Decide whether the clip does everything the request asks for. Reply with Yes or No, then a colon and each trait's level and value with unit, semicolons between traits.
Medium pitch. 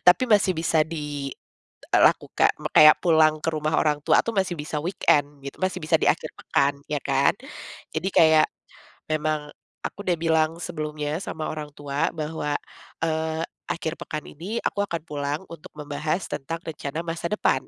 Yes: medium, 155 Hz